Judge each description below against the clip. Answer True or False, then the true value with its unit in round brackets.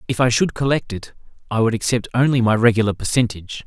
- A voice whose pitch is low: True (115 Hz)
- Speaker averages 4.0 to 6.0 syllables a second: False (6.5 syllables/s)